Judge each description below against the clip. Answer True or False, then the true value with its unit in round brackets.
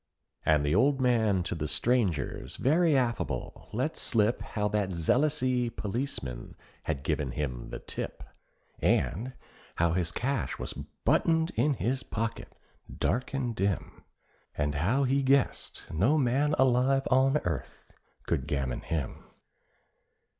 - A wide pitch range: True (8.3 semitones)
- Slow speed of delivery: True (130 wpm)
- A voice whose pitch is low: True (115 Hz)